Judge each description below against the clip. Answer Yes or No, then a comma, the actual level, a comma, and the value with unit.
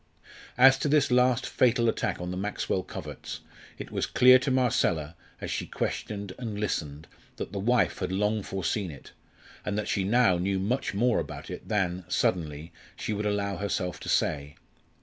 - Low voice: Yes, low, 100 Hz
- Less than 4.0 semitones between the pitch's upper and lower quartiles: No, average, 4.9 semitones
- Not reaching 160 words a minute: No, average, 175 wpm